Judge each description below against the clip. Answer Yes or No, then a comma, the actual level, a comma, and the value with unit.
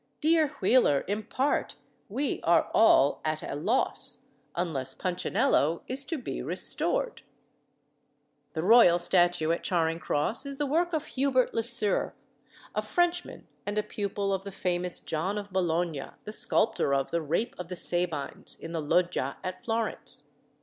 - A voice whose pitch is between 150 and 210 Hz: Yes, high, 190 Hz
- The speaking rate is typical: Yes, average, 150 wpm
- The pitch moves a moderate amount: No, wide, 6.2 semitones